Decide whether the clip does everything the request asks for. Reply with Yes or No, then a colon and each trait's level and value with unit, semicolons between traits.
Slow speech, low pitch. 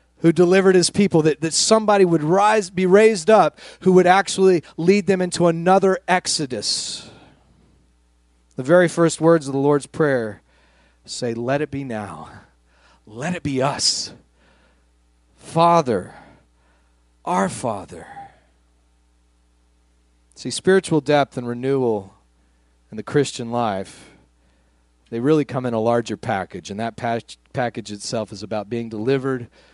Yes: slow, 130 wpm; low, 120 Hz